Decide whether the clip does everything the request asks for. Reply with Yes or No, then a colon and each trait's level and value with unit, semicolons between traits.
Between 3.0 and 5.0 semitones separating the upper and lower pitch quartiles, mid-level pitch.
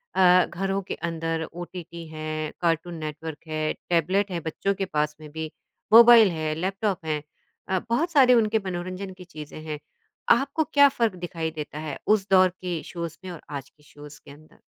Yes: average, 3.8 semitones; medium, 170 Hz